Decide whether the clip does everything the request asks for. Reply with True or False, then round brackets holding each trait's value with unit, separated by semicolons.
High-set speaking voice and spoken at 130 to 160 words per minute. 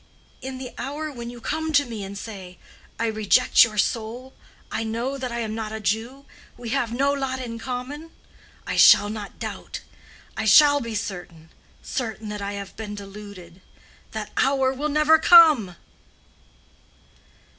True (230 Hz; 155 wpm)